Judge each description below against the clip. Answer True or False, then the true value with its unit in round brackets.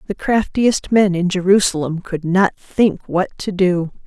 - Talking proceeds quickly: False (160 wpm)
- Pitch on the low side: False (185 Hz)